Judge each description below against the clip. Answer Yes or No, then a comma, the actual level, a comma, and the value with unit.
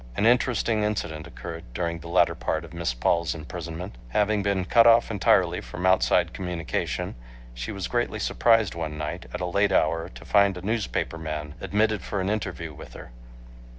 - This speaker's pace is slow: No, average, 180 wpm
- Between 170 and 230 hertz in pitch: No, very low, 90 Hz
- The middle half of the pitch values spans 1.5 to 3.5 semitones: No, average, 4.1 semitones